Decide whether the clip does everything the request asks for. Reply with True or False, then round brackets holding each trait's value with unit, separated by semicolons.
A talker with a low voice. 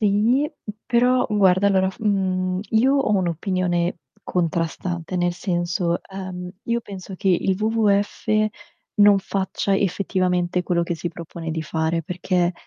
False (185 Hz)